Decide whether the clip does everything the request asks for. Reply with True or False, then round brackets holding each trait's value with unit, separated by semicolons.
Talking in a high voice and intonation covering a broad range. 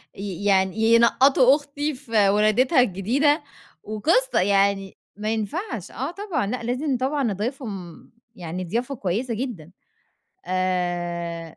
True (215 Hz; 5.8 semitones)